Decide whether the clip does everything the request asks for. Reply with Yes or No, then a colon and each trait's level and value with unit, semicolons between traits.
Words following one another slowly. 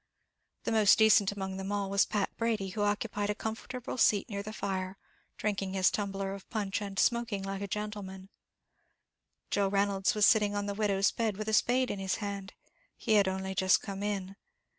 No: average, 190 wpm